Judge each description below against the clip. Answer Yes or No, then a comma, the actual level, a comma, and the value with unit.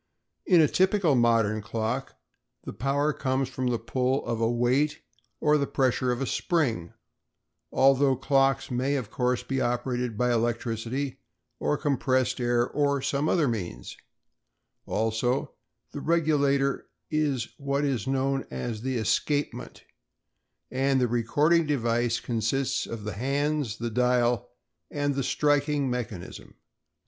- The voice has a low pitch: Yes, low, 130 Hz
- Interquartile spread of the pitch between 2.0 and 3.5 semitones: Yes, average, 3.1 semitones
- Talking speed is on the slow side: Yes, slow, 130 wpm